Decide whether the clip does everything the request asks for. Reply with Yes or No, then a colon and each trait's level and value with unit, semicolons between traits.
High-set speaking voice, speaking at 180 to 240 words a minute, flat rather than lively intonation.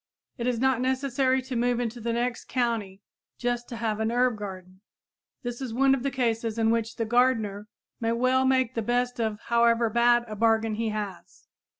Yes: high, 235 Hz; average, 195 wpm; narrow, 1.9 semitones